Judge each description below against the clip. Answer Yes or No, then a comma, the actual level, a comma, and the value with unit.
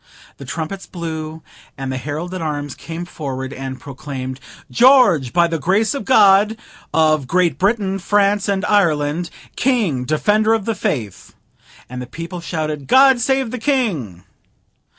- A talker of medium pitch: Yes, medium, 170 Hz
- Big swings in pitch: Yes, wide, 6.2 semitones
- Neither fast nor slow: Yes, average, 150 wpm